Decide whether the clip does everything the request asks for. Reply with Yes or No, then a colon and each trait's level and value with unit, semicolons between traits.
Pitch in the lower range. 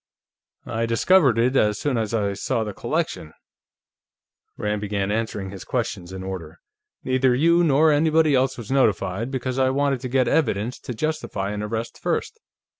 Yes: low, 115 Hz